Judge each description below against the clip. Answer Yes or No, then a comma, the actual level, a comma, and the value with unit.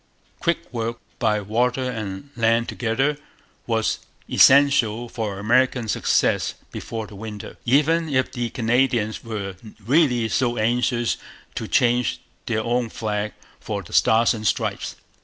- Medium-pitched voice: No, low, 115 Hz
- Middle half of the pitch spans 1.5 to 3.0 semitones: Yes, narrow, 2.4 semitones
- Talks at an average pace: No, slow, 130 wpm